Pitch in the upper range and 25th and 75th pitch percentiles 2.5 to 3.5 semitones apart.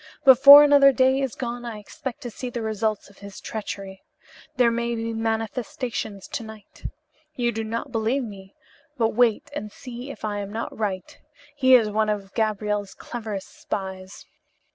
Yes: high, 225 Hz; average, 3.1 semitones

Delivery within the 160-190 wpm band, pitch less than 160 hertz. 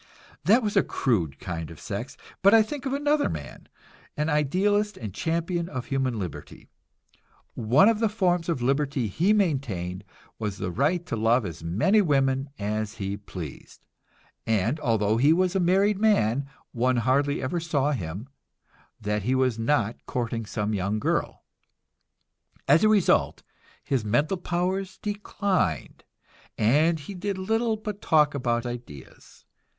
No: average, 150 wpm; medium, 140 Hz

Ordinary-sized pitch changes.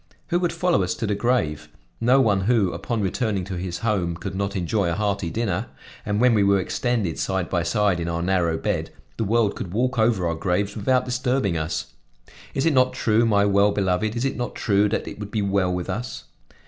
Yes: average, 4.2 semitones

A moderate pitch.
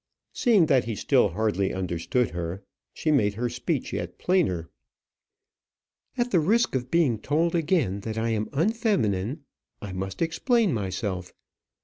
No: low, 120 Hz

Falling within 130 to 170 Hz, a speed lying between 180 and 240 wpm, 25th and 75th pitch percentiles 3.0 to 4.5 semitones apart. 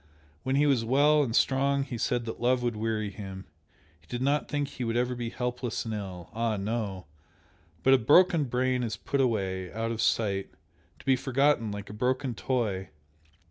No: low, 120 Hz; average, 190 wpm; average, 3.6 semitones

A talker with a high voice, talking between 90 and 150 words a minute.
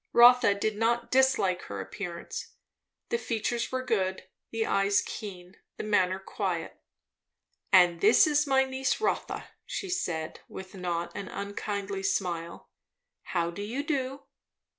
Yes: high, 205 Hz; slow, 135 wpm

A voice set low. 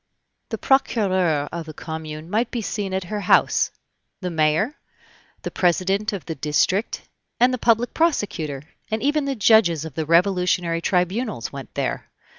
No: medium, 185 Hz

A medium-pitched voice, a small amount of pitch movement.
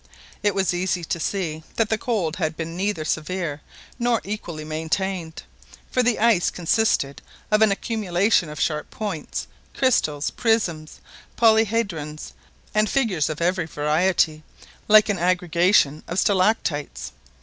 No: medium, 180 Hz; average, 5.2 semitones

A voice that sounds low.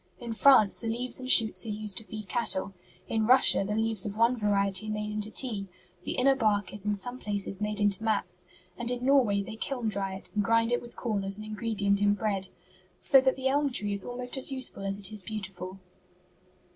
No: high, 215 Hz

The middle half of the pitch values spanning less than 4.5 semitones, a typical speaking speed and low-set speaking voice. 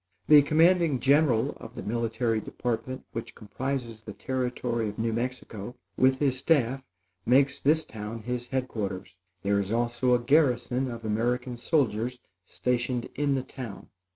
Yes: average, 2.7 semitones; average, 150 wpm; low, 125 Hz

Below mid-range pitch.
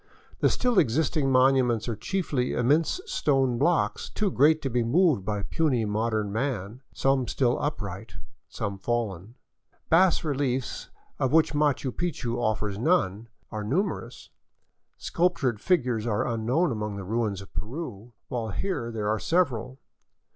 Yes: low, 125 Hz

